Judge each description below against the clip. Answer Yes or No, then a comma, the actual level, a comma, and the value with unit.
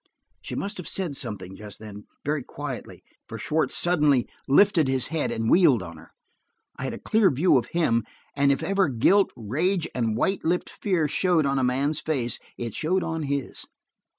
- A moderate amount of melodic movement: No, wide, 6.0 semitones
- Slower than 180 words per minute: No, average, 185 wpm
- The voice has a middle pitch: Yes, medium, 145 Hz